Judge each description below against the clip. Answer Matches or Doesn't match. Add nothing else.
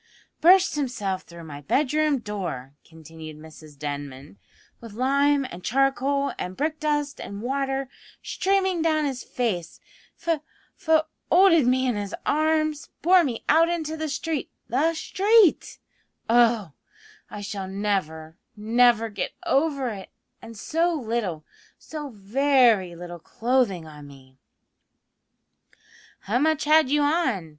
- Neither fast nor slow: Doesn't match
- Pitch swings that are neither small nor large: Doesn't match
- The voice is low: Doesn't match